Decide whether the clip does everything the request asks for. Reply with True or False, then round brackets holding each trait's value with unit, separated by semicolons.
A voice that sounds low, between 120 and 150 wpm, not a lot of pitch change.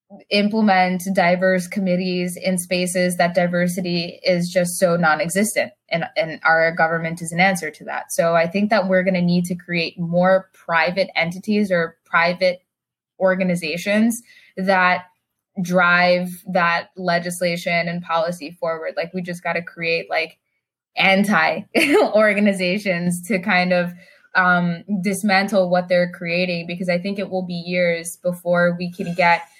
False (180 Hz; 145 wpm; 1.6 semitones)